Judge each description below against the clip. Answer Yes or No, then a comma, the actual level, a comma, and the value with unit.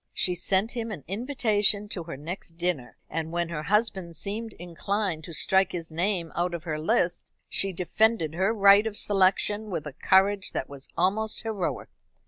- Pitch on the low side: No, high, 190 Hz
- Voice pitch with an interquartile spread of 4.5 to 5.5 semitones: No, average, 3.6 semitones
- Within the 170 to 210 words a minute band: Yes, average, 175 wpm